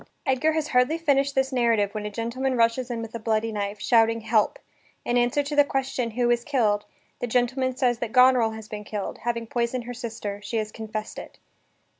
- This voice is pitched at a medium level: No, high, 235 Hz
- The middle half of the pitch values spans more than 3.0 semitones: No, average, 2.7 semitones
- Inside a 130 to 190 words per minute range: No, fast, 205 wpm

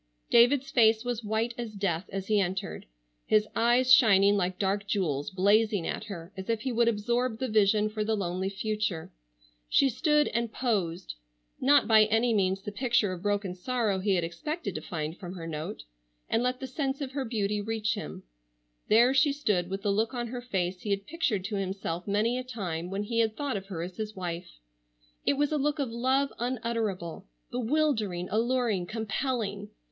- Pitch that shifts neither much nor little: Yes, average, 4.1 semitones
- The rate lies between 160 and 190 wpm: Yes, average, 185 wpm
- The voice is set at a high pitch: Yes, high, 215 Hz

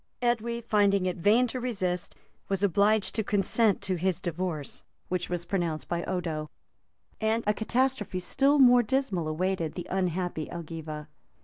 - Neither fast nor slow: Yes, average, 155 wpm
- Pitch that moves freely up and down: No, average, 4.3 semitones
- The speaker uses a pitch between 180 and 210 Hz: Yes, high, 190 Hz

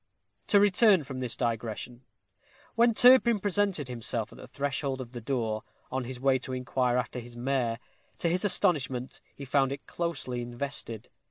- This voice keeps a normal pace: Yes, average, 165 wpm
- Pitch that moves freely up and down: Yes, wide, 5.7 semitones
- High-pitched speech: No, low, 130 Hz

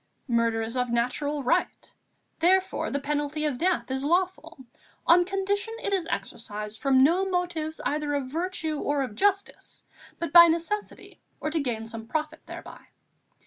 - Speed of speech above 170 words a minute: No, average, 155 wpm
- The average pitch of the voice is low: No, very high, 305 Hz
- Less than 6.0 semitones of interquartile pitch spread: Yes, wide, 5.5 semitones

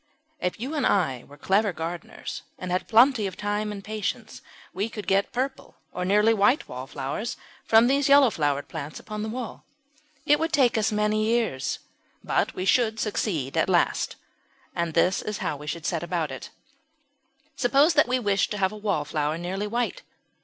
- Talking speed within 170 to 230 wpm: Yes, average, 180 wpm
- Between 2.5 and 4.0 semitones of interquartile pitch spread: No, average, 5.3 semitones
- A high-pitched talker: Yes, high, 205 Hz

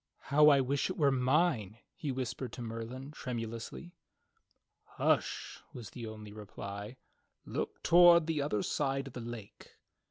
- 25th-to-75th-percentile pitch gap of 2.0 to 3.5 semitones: No, average, 4.3 semitones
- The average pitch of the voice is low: Yes, low, 130 Hz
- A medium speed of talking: Yes, average, 150 wpm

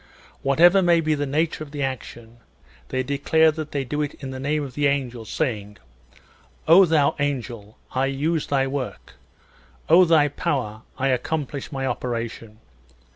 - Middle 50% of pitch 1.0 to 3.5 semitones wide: Yes, average, 3.2 semitones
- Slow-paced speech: No, average, 165 wpm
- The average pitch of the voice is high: No, medium, 140 Hz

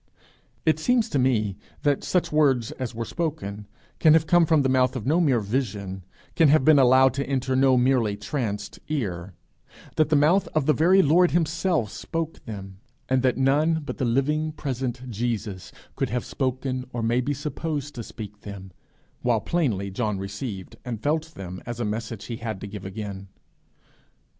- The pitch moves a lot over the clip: Yes, wide, 6.0 semitones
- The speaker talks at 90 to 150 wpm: No, average, 180 wpm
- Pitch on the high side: No, low, 130 Hz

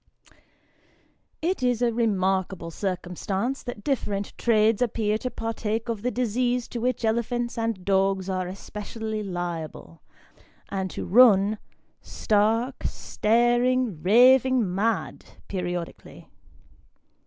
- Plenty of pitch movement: No, average, 3.9 semitones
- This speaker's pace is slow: Yes, slow, 105 wpm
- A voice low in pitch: No, high, 220 Hz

